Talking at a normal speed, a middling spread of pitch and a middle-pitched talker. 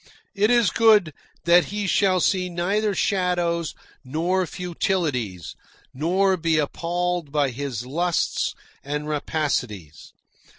No: slow, 110 wpm; average, 4.2 semitones; medium, 170 Hz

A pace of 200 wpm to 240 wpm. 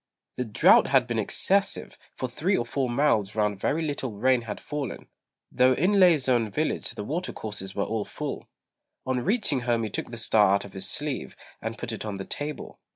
Yes: fast, 205 wpm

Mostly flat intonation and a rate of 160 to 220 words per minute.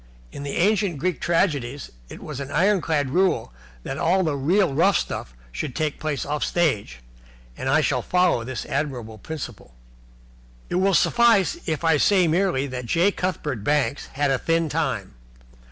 No: average, 5.0 semitones; average, 165 wpm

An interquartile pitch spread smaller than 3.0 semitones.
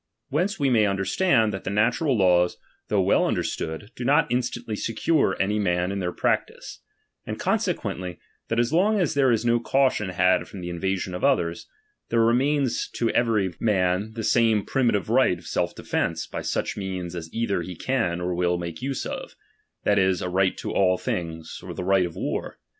No: average, 5.0 semitones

